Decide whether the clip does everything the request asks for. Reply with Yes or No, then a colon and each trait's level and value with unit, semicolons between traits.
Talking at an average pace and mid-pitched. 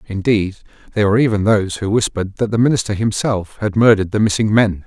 No: average, 195 wpm; low, 105 Hz